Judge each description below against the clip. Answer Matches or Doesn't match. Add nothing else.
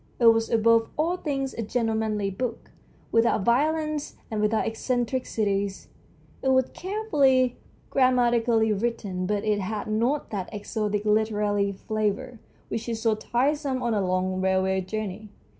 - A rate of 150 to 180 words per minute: Doesn't match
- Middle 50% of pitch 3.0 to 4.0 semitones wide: Matches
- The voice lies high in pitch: Matches